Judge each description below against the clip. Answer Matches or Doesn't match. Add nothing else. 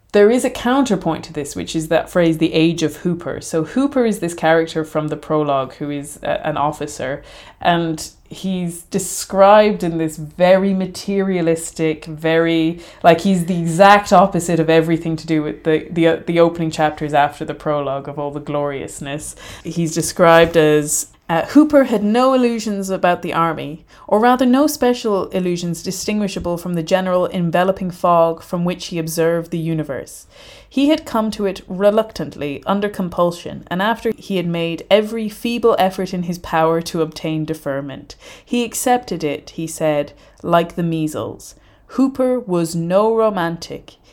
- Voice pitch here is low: Doesn't match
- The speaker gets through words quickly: Doesn't match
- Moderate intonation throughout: Matches